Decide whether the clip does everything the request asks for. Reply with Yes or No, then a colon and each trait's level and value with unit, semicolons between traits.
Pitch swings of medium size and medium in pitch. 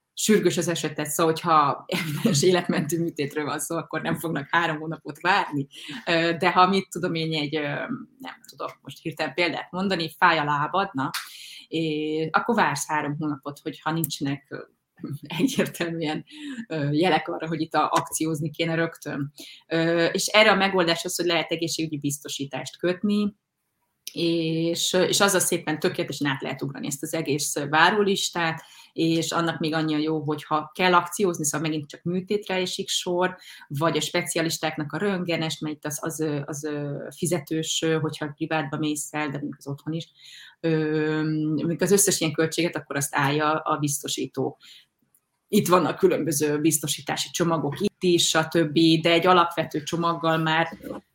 No: narrow, 2.3 semitones; medium, 160 Hz